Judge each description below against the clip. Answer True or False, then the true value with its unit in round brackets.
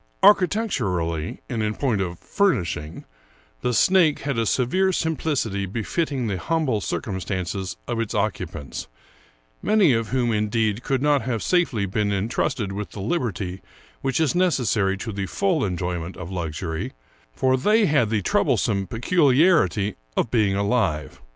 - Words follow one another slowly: False (145 wpm)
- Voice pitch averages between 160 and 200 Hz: False (110 Hz)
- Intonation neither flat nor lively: False (6.8 semitones)